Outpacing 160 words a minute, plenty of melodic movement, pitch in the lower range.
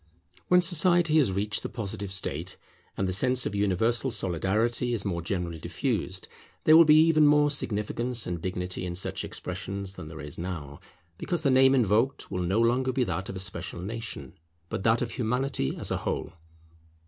Yes: average, 185 wpm; wide, 5.9 semitones; low, 105 Hz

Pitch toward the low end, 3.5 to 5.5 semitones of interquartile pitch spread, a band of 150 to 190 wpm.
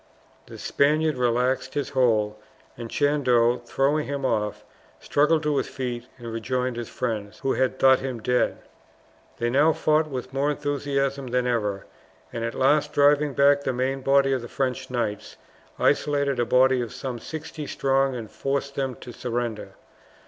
No: low, 130 Hz; average, 2.7 semitones; average, 165 wpm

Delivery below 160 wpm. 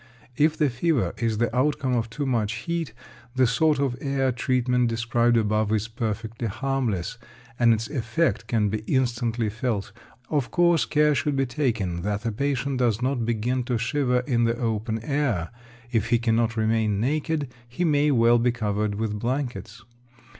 No: average, 170 wpm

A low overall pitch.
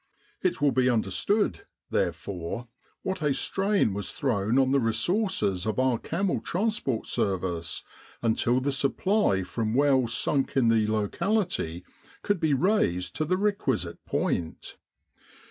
Yes: low, 130 Hz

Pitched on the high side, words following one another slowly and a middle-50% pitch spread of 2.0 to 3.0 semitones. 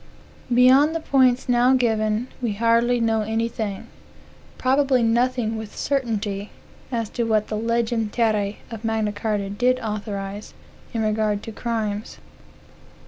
Yes: high, 225 Hz; slow, 130 wpm; narrow, 2.4 semitones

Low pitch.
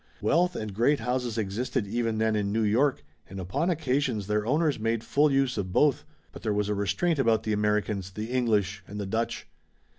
Yes: low, 110 Hz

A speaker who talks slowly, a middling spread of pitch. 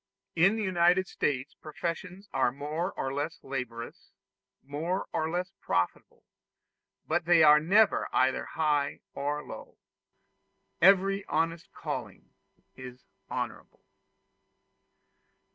Yes: slow, 105 wpm; average, 4.4 semitones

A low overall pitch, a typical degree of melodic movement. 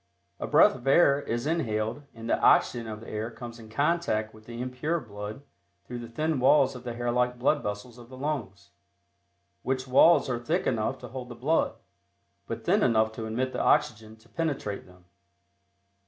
Yes: low, 120 Hz; average, 3.6 semitones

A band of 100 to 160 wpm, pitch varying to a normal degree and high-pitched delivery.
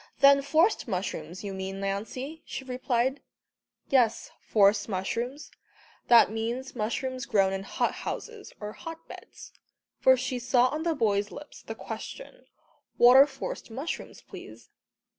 Yes: average, 140 wpm; average, 5.0 semitones; high, 245 Hz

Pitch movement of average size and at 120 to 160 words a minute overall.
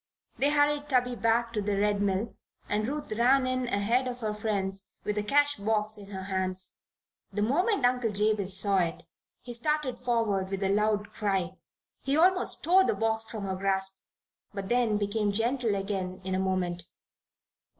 No: average, 4.0 semitones; average, 175 wpm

